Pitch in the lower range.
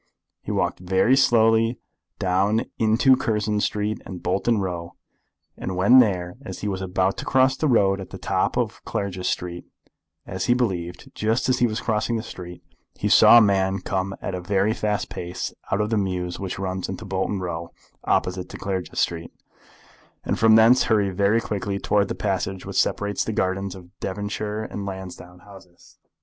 Yes: low, 100 Hz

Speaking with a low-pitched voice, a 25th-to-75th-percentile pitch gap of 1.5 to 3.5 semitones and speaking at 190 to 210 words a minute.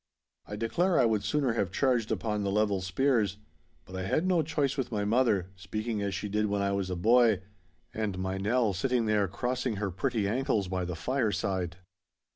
No: low, 105 Hz; average, 4.2 semitones; average, 195 wpm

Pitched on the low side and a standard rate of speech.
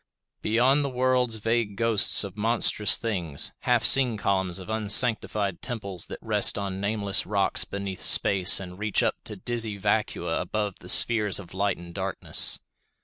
Yes: low, 105 Hz; average, 155 wpm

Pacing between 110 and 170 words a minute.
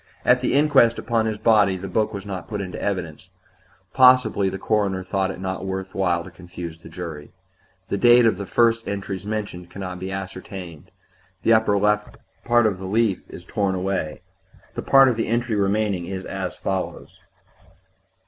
No: average, 185 wpm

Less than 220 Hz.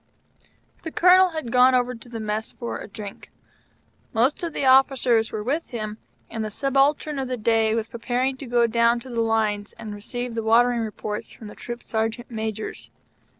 No: high, 235 Hz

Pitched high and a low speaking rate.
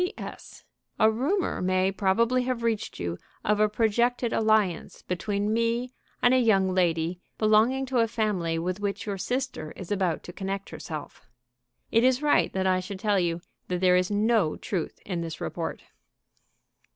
No: high, 205 Hz; average, 165 wpm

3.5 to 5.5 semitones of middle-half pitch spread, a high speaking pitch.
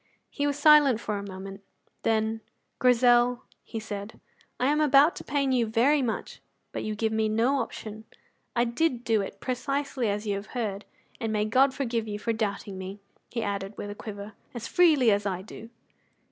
Yes: average, 3.8 semitones; high, 225 Hz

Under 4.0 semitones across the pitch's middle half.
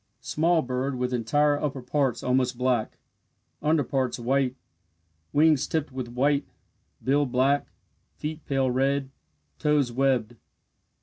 Yes: narrow, 2.4 semitones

